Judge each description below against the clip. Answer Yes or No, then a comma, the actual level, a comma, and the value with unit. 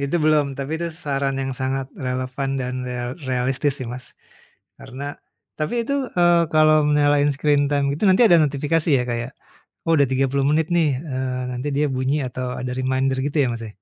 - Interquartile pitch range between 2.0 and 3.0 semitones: Yes, average, 2.7 semitones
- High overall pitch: No, medium, 140 Hz